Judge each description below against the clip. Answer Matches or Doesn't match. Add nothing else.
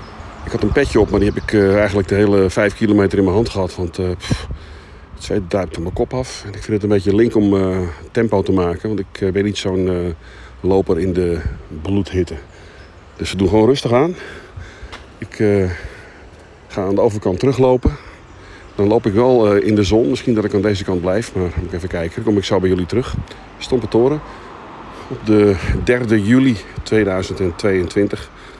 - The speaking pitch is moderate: Doesn't match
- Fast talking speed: Matches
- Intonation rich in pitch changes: Doesn't match